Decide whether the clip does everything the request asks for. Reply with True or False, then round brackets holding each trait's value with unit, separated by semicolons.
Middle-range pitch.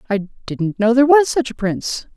False (235 Hz)